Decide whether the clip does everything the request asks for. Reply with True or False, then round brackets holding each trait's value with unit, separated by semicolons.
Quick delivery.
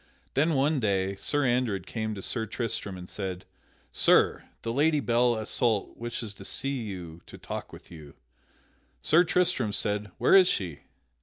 False (160 wpm)